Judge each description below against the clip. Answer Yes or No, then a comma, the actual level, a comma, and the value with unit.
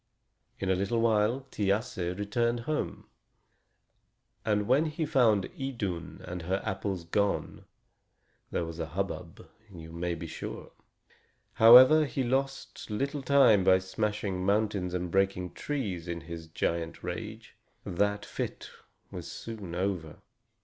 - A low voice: Yes, low, 100 Hz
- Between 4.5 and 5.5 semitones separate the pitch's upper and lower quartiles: Yes, average, 4.8 semitones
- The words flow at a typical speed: No, slow, 130 wpm